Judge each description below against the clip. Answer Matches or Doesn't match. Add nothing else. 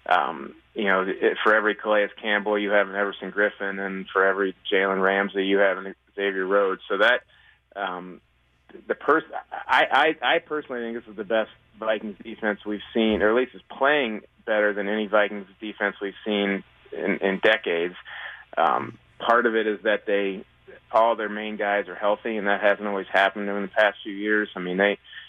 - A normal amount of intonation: Doesn't match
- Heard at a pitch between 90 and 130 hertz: Matches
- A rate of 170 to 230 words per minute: Matches